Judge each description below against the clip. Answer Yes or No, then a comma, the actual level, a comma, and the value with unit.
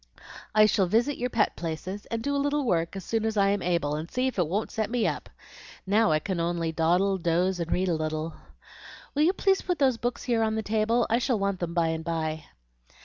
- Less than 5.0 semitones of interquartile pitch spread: No, wide, 5.4 semitones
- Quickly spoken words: Yes, fast, 240 wpm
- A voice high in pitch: Yes, high, 200 Hz